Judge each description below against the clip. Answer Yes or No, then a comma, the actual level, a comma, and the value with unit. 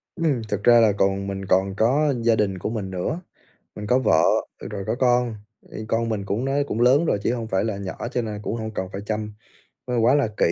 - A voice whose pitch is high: No, low, 110 Hz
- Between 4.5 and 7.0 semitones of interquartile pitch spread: No, average, 3.7 semitones